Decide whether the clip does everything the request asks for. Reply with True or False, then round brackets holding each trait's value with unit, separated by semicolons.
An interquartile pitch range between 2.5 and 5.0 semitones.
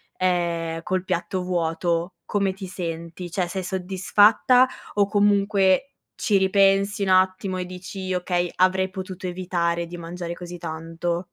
False (1.8 semitones)